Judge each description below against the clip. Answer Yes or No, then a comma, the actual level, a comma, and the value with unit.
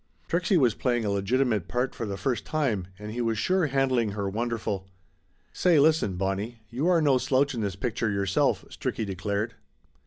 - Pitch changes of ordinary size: Yes, average, 5.0 semitones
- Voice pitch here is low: Yes, low, 115 Hz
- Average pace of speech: Yes, average, 190 wpm